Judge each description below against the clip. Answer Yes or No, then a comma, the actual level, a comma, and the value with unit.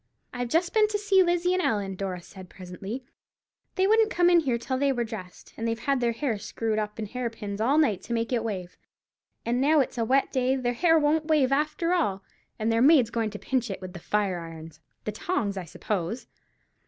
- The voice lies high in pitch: Yes, high, 235 Hz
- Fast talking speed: Yes, fast, 220 wpm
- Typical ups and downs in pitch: No, wide, 6.4 semitones